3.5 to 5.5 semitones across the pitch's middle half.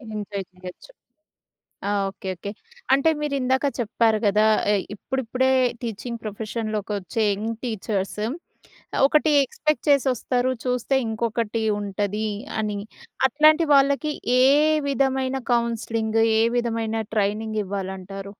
Yes: average, 4.0 semitones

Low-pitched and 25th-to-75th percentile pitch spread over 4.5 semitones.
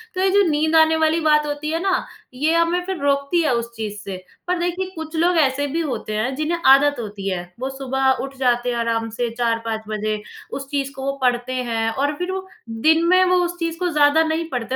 No: very high, 285 Hz; average, 5.2 semitones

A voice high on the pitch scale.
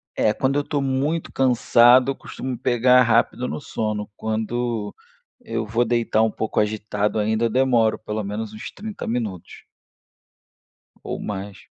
No: low, 115 Hz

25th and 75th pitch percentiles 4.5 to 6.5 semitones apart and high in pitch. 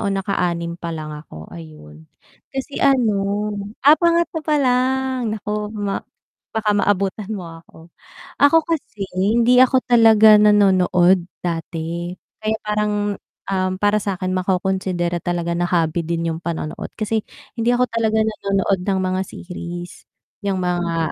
No: average, 4.0 semitones; high, 195 Hz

